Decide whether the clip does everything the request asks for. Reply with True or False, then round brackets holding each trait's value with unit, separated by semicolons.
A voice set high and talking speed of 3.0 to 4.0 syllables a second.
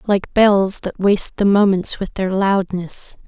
True (195 Hz; 3.9 syllables/s)